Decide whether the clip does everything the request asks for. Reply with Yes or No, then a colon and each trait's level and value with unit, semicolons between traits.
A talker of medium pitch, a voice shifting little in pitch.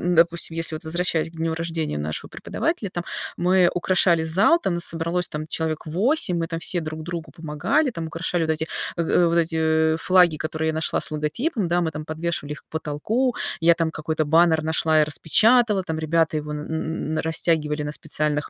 Yes: medium, 160 Hz; narrow, 1.7 semitones